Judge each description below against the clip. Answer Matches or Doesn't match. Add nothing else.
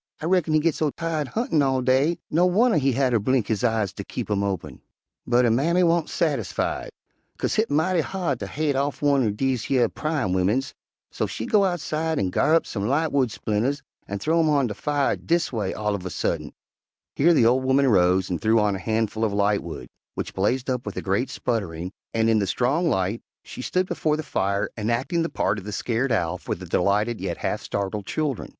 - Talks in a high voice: Doesn't match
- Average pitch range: Doesn't match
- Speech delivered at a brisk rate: Matches